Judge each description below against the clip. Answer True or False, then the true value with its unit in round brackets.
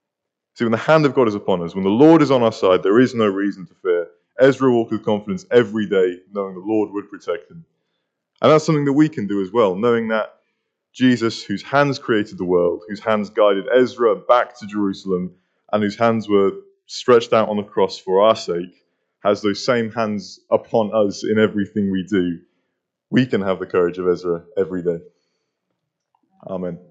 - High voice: False (105 Hz)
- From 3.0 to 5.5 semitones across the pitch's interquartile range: True (4.0 semitones)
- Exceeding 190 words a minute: True (200 wpm)